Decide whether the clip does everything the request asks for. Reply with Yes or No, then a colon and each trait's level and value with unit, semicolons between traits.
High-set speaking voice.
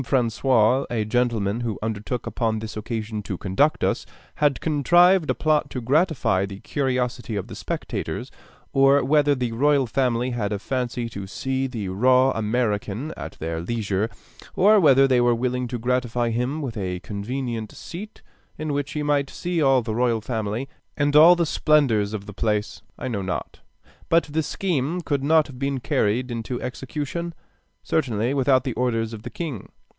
No: low, 125 Hz